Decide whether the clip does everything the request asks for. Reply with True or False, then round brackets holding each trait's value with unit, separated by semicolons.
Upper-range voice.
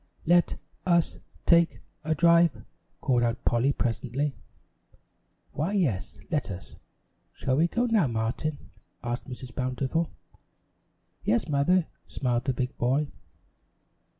False (140 Hz)